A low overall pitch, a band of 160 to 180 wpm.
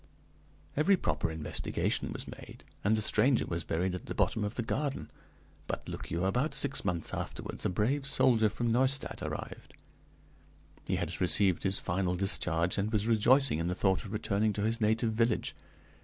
Yes: low, 105 Hz; average, 175 wpm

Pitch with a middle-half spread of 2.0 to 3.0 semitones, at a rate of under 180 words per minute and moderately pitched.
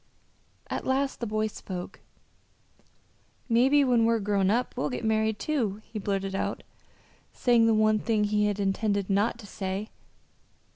No: narrow, 2.5 semitones; average, 150 wpm; high, 215 Hz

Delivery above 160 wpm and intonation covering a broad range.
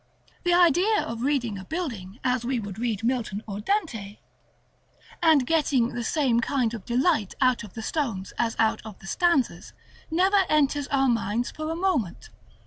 Yes: average, 170 wpm; wide, 5.8 semitones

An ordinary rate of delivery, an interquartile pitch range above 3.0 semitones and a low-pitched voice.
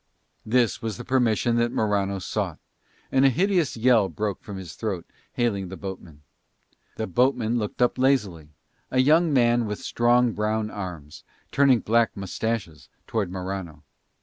Yes: average, 150 wpm; average, 4.1 semitones; low, 110 Hz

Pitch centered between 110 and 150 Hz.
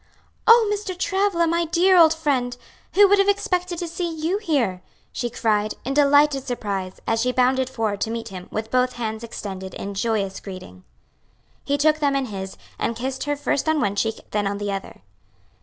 No: very high, 255 Hz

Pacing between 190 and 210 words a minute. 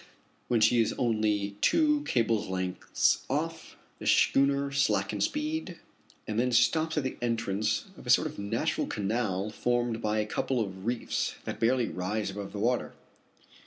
No: average, 160 wpm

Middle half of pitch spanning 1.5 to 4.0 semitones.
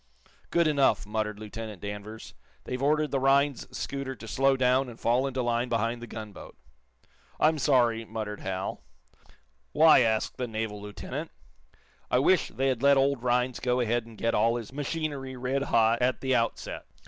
Yes: average, 3.3 semitones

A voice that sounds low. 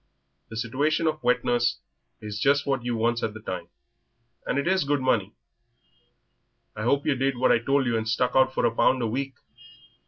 Yes: low, 125 Hz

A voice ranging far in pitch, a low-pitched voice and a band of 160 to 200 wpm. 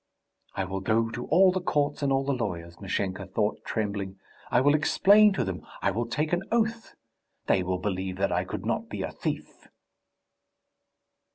Yes: wide, 7.7 semitones; low, 115 Hz; average, 180 wpm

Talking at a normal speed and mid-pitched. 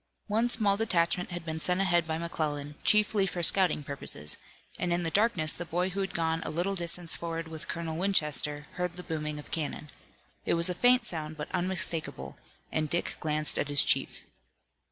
Yes: average, 190 wpm; medium, 170 Hz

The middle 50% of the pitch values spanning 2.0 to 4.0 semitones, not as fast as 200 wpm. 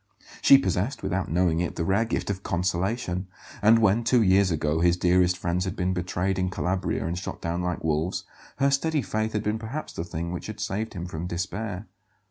No: average, 3.7 semitones; fast, 205 wpm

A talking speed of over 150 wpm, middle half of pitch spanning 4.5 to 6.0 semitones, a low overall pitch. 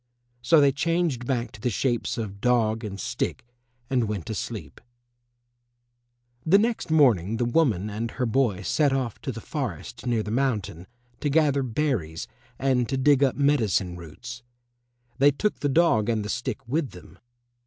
Yes: average, 165 wpm; average, 4.8 semitones; low, 125 Hz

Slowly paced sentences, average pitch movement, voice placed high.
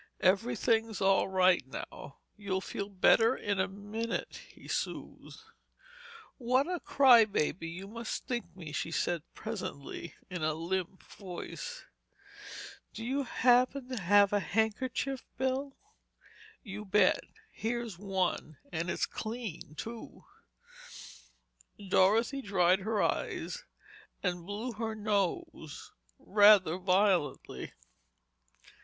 Yes: slow, 105 wpm; average, 4.0 semitones; high, 205 Hz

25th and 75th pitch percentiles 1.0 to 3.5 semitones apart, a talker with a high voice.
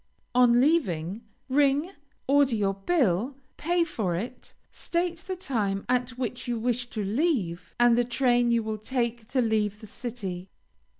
No: average, 4.2 semitones; high, 240 Hz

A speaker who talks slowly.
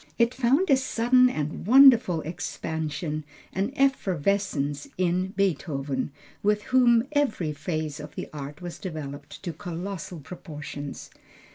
Yes: slow, 120 wpm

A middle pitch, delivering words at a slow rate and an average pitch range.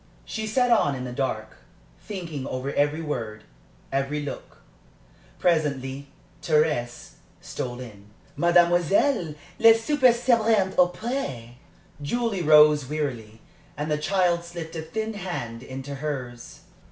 No: medium, 150 Hz; slow, 120 wpm; wide, 6.1 semitones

